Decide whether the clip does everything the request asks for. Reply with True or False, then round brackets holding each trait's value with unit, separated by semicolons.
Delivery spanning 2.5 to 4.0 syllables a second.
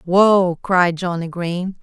True (3.1 syllables/s)